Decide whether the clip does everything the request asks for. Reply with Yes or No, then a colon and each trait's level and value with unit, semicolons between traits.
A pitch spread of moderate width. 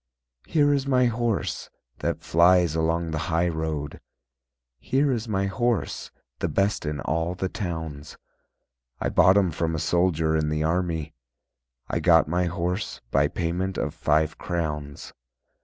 Yes: average, 3.4 semitones